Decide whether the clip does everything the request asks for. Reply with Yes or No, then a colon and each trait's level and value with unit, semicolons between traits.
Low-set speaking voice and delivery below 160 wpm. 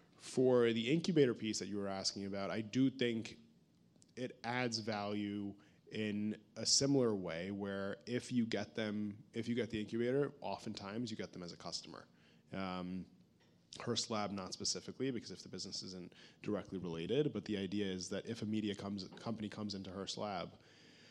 No: low, 105 Hz; average, 180 wpm